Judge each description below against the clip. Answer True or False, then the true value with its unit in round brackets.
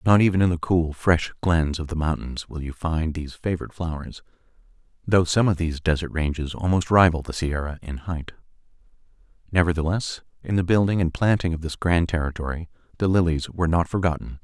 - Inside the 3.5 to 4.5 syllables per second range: False (5.8 syllables/s)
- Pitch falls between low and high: False (85 Hz)